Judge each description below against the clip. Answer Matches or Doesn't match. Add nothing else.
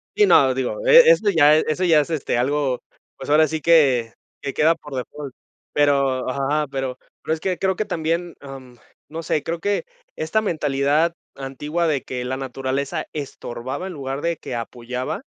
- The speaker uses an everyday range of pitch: Matches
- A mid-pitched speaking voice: Matches